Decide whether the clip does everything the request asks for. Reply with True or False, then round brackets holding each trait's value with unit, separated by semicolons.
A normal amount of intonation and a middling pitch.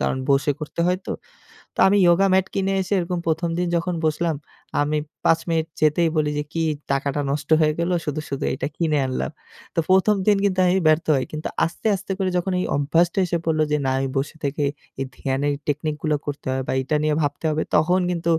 True (3.1 semitones; 155 Hz)